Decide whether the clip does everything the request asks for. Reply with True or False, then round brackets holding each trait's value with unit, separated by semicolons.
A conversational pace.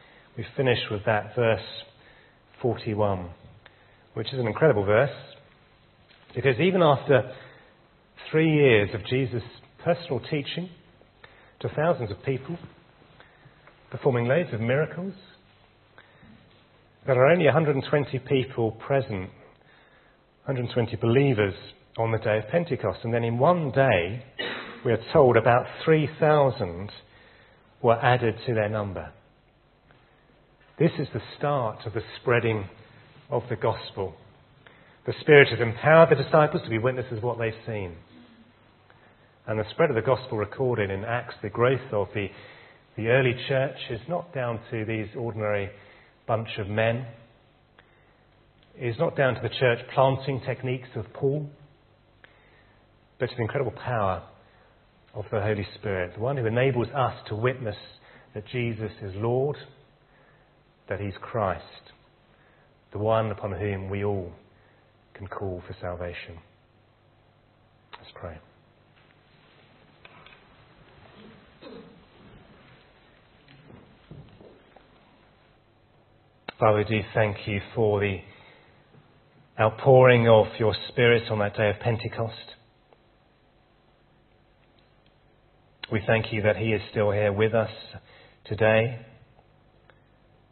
False (115 wpm)